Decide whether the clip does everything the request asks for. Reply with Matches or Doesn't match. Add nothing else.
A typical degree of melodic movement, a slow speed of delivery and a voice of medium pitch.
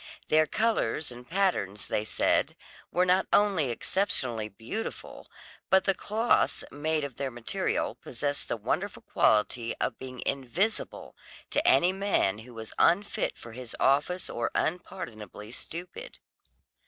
Doesn't match